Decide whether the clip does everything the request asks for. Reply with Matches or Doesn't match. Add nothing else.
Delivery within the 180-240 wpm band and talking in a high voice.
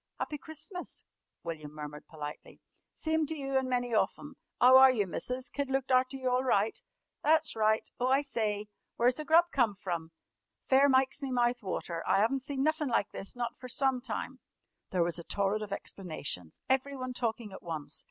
Matches